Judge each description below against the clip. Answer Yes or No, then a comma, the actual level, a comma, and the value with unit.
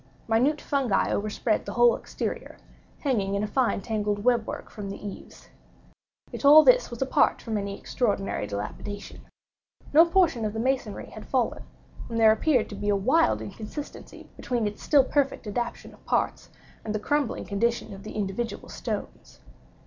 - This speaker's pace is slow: No, average, 165 wpm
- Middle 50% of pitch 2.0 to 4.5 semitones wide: Yes, average, 4.2 semitones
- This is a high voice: Yes, high, 225 Hz